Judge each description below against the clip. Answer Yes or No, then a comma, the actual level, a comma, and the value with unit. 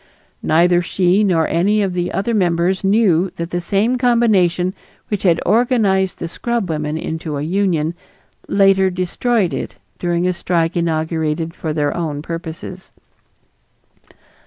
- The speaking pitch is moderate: Yes, medium, 180 Hz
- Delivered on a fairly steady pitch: No, average, 3.0 semitones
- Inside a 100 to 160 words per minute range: Yes, slow, 135 wpm